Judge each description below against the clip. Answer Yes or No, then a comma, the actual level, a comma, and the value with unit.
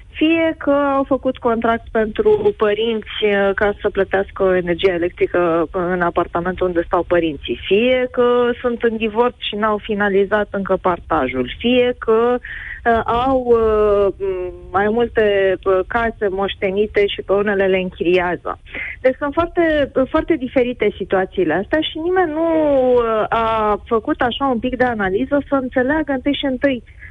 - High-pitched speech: Yes, high, 225 Hz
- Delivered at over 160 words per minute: No, average, 135 wpm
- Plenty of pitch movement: No, average, 4.9 semitones